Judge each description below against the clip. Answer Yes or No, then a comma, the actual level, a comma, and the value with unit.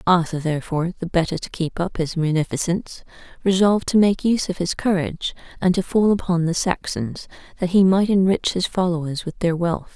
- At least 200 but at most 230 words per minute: No, average, 185 wpm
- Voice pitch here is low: No, medium, 175 Hz